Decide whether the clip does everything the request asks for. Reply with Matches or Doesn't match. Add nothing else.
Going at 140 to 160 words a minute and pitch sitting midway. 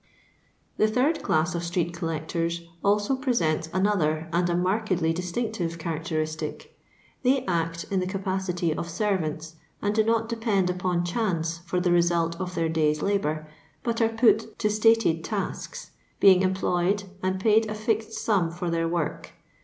Matches